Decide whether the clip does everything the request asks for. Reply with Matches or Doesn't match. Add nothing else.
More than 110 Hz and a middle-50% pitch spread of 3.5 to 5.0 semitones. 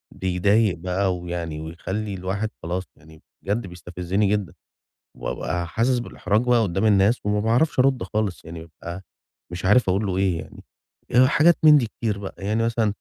Doesn't match